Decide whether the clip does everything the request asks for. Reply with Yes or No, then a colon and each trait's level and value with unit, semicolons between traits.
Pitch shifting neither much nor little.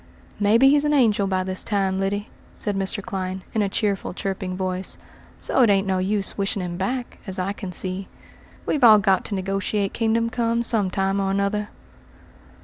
No: narrow, 2.2 semitones